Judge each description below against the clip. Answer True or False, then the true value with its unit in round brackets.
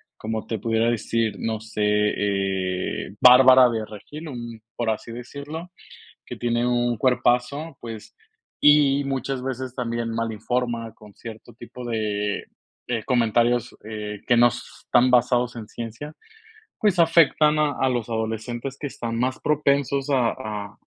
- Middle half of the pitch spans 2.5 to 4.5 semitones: True (2.8 semitones)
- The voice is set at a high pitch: False (120 Hz)